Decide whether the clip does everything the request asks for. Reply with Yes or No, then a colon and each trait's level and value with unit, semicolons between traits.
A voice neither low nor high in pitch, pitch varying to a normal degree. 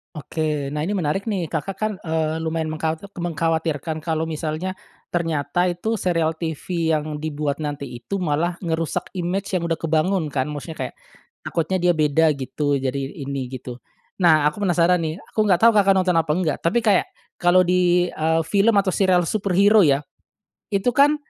Yes: medium, 165 Hz; average, 3.1 semitones